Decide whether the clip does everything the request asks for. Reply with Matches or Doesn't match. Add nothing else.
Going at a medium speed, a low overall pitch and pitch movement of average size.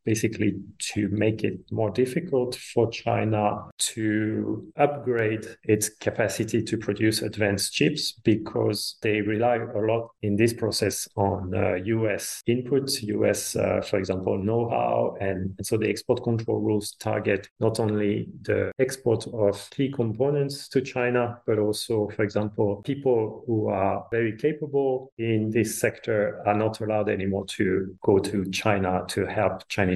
Doesn't match